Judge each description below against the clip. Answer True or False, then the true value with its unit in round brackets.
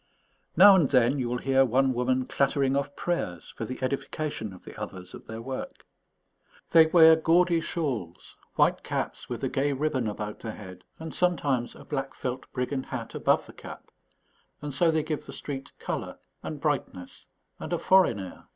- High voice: False (135 Hz)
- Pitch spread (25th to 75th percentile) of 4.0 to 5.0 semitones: True (4.3 semitones)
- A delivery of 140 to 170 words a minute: False (180 wpm)